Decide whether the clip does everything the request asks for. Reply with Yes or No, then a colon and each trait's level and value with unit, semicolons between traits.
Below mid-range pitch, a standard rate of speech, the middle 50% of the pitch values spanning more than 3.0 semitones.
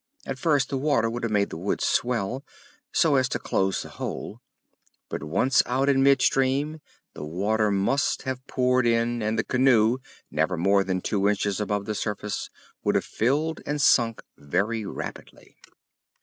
Yes: low, 115 Hz; average, 170 wpm; average, 4.7 semitones